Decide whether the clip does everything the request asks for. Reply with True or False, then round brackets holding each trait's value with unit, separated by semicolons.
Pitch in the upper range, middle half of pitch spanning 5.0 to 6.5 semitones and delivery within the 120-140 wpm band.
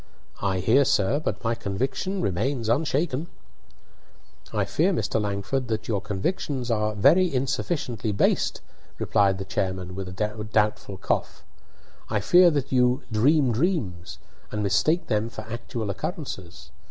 False (110 Hz; 5.4 semitones; 135 wpm)